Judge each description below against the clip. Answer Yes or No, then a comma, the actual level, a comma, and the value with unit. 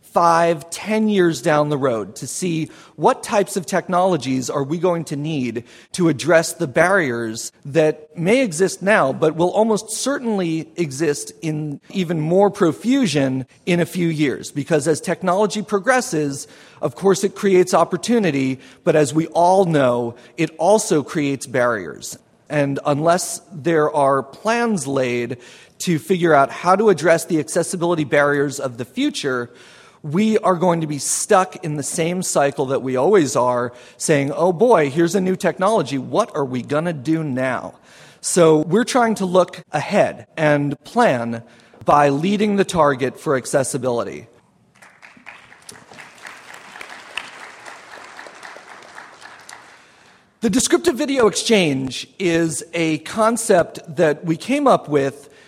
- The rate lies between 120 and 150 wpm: Yes, average, 140 wpm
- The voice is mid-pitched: Yes, medium, 165 Hz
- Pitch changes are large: No, average, 4.8 semitones